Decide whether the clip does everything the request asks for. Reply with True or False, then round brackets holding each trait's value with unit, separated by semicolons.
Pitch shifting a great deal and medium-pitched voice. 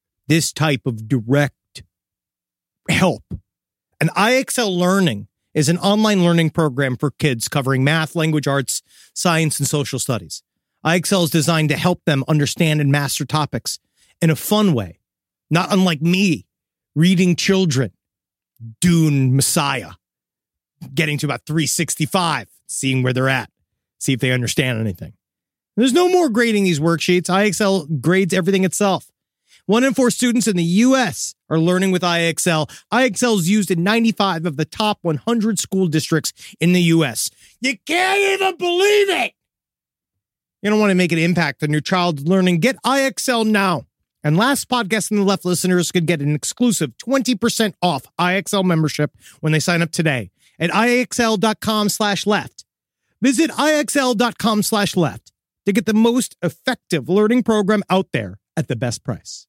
True (6.3 semitones; 175 Hz)